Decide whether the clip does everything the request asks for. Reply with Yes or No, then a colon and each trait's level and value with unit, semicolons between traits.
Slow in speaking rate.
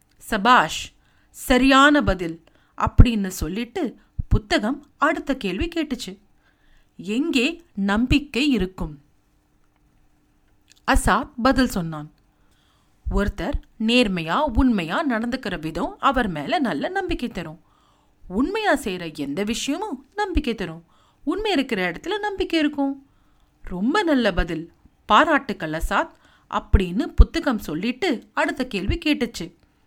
Yes: slow, 95 wpm